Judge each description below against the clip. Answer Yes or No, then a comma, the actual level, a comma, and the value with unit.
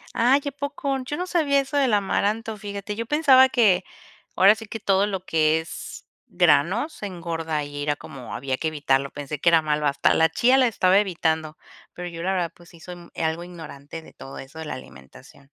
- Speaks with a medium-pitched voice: Yes, medium, 175 Hz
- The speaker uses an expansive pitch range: Yes, wide, 6.2 semitones